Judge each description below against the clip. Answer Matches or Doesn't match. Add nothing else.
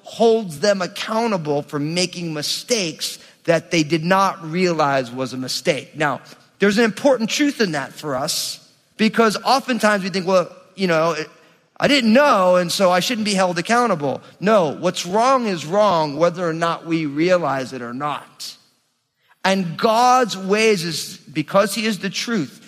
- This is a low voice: Doesn't match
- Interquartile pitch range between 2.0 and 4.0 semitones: Doesn't match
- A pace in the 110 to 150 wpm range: Doesn't match